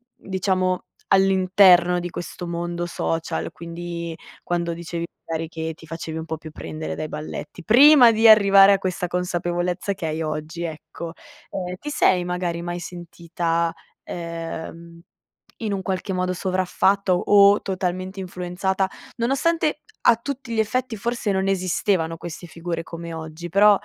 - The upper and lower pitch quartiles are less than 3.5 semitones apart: Yes, narrow, 2.6 semitones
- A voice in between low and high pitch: Yes, medium, 180 Hz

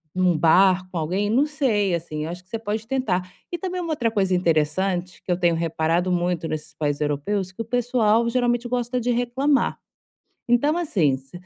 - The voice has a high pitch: Yes, high, 195 Hz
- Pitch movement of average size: No, wide, 5.9 semitones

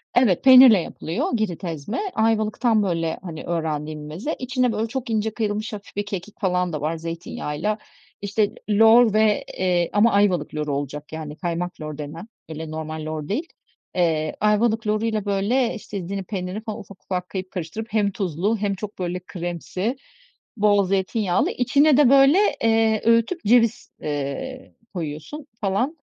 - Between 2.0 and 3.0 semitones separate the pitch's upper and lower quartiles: No, average, 5.0 semitones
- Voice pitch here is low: No, high, 200 Hz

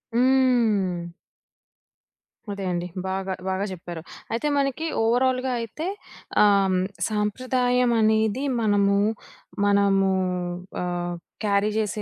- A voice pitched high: Yes, high, 210 Hz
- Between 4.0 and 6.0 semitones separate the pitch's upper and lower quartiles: Yes, average, 4.3 semitones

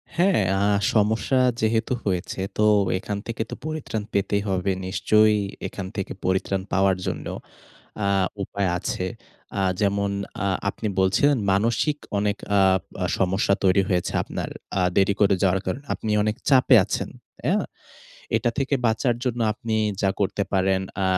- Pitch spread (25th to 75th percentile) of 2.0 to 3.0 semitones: Yes, average, 2.7 semitones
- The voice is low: Yes, low, 100 Hz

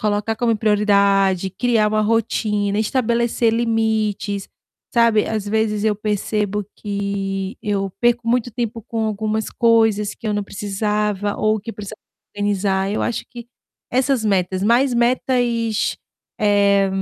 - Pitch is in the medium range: No, high, 210 Hz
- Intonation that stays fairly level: Yes, narrow, 2.0 semitones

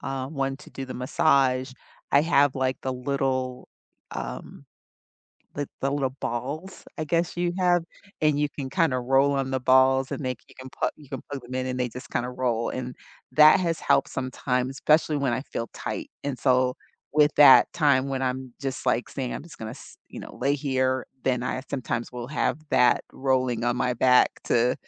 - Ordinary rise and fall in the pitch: No, narrow, 2.0 semitones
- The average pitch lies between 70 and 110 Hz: No, low, 130 Hz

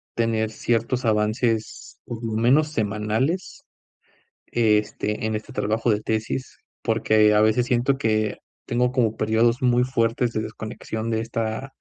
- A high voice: No, low, 115 Hz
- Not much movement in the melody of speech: Yes, narrow, 2.0 semitones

